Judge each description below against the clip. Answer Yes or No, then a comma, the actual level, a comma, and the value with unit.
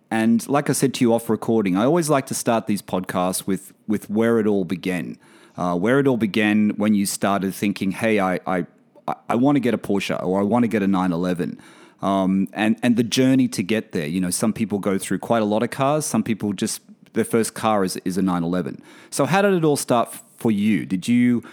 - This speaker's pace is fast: Yes, fast, 235 wpm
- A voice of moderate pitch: No, low, 110 Hz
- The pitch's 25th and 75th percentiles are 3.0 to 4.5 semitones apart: Yes, average, 3.8 semitones